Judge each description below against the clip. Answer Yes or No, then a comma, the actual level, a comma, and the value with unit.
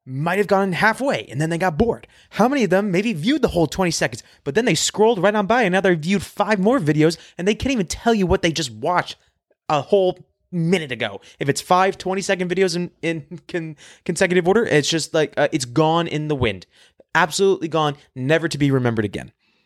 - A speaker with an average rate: No, fast, 225 wpm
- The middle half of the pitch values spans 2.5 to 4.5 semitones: Yes, average, 4.2 semitones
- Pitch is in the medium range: Yes, medium, 175 Hz